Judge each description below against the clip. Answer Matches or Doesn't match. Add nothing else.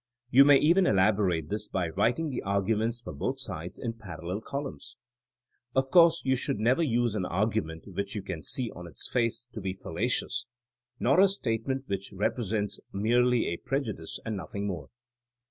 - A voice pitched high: Doesn't match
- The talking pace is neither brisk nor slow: Matches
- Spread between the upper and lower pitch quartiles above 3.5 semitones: Matches